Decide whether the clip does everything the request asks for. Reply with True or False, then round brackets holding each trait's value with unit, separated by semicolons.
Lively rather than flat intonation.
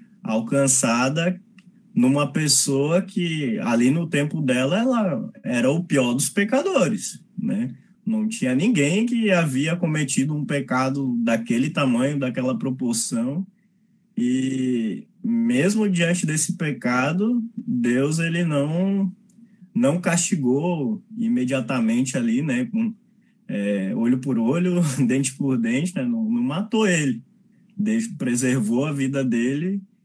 True (8.2 semitones)